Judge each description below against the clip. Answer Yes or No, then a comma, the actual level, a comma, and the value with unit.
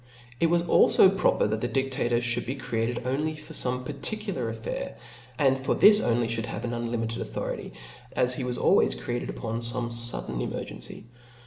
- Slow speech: No, average, 175 wpm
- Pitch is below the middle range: Yes, low, 120 Hz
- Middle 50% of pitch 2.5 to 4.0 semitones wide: Yes, average, 2.8 semitones